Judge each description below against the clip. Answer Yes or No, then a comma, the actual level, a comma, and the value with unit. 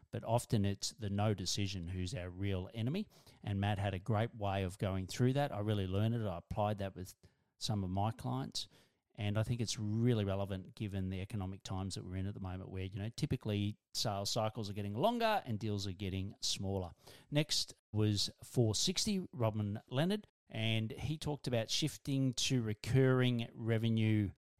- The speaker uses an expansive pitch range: No, average, 3.4 semitones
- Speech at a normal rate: Yes, average, 185 wpm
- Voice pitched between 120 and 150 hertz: No, low, 105 Hz